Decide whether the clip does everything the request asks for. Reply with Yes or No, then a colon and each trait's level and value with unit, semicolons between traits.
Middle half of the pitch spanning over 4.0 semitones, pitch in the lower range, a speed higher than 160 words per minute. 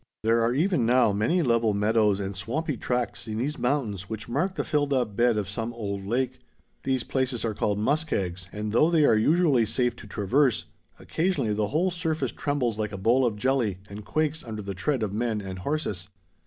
Yes: average, 5.2 semitones; low, 115 Hz; average, 200 wpm